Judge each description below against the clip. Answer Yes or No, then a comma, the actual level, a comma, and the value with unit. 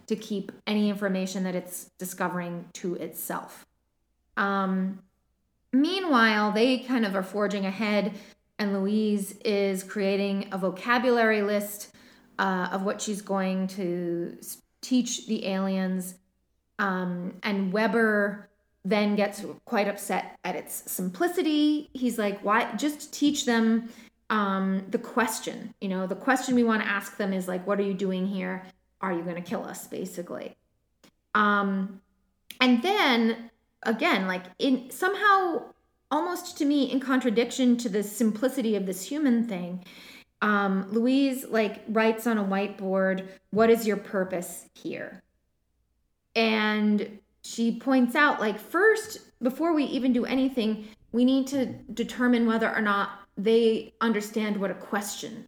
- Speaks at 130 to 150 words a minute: Yes, average, 140 wpm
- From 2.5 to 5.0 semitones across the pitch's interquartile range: Yes, average, 3.7 semitones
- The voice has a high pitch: Yes, high, 210 Hz